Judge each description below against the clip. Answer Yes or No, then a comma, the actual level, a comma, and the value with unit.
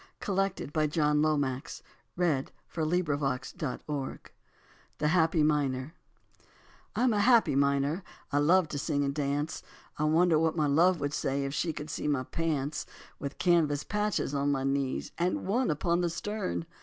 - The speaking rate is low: No, average, 165 wpm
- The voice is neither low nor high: Yes, medium, 150 Hz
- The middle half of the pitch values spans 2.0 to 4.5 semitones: Yes, average, 3.4 semitones